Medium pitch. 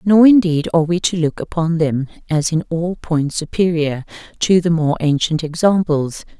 Yes: medium, 165 Hz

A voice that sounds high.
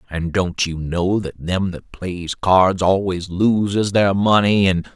No: very low, 95 Hz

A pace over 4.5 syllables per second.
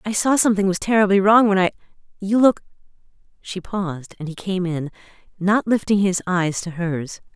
Yes: 5.3 syllables/s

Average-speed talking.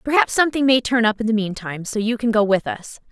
No: fast, 270 wpm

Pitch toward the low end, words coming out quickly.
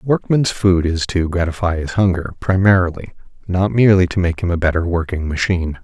No: very low, 90 Hz; average, 185 wpm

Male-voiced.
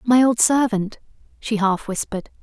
No: female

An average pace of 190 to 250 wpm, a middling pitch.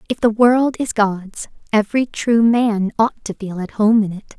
No: fast, 205 wpm; high, 220 Hz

